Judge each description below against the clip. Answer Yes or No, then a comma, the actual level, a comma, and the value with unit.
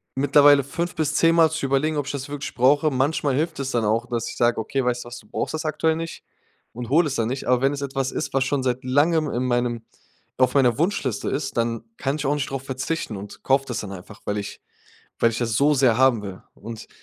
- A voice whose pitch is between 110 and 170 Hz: Yes, low, 135 Hz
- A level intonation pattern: No, average, 3.4 semitones